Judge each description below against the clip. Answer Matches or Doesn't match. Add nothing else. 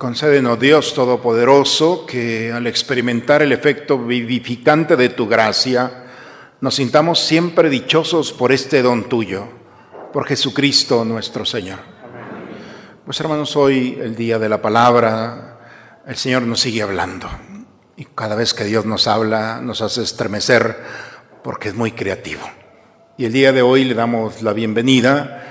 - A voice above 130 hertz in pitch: Doesn't match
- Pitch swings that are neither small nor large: Matches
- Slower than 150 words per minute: Matches